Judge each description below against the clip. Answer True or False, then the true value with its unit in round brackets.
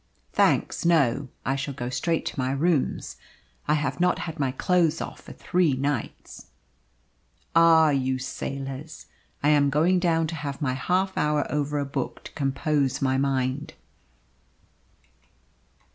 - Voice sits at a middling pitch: True (145 Hz)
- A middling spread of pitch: True (3.2 semitones)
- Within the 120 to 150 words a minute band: True (145 wpm)